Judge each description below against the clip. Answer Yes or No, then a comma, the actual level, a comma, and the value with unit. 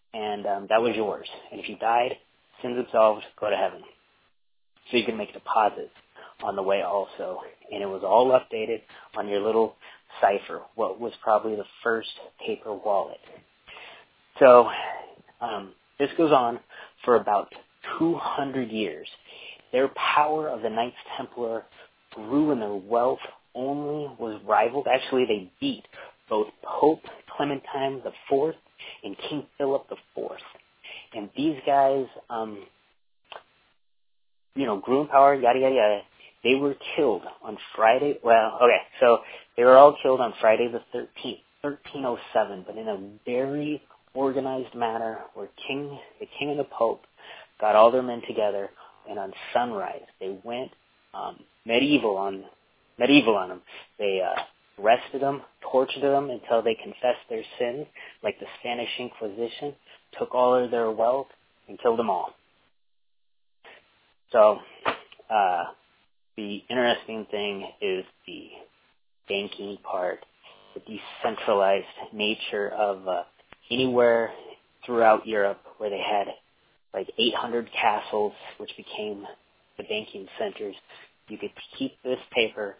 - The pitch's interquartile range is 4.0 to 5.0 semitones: Yes, average, 4.3 semitones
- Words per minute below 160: Yes, average, 140 wpm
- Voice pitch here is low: Yes, low, 120 Hz